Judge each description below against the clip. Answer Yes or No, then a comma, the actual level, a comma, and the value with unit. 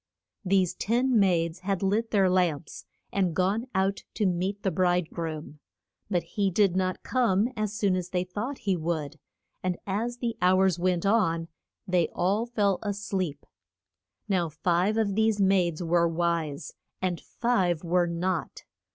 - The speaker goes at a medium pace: Yes, average, 155 wpm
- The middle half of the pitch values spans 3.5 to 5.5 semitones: No, average, 2.8 semitones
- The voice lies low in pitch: No, medium, 185 Hz